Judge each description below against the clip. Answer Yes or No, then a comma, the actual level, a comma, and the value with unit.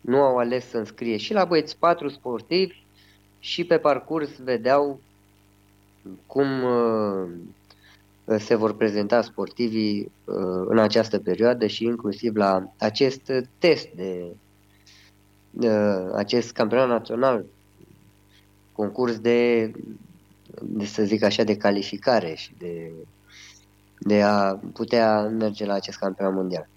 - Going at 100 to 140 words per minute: Yes, slow, 115 wpm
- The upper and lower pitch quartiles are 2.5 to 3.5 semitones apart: Yes, average, 3.1 semitones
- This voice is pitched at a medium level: No, low, 105 Hz